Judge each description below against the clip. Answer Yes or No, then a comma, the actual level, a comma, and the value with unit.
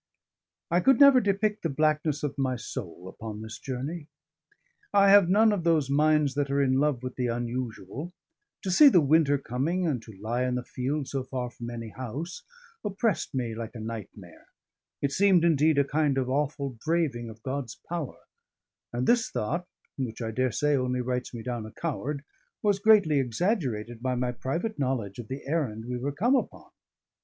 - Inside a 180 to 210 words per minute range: Yes, average, 185 wpm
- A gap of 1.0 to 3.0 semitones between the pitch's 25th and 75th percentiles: No, average, 5.2 semitones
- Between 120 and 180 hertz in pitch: Yes, low, 135 Hz